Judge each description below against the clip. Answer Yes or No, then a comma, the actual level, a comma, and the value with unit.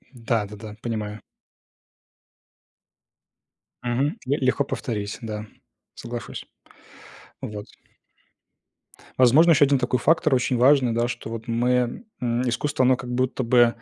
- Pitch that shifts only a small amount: Yes, narrow, 2.0 semitones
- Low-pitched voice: Yes, low, 120 Hz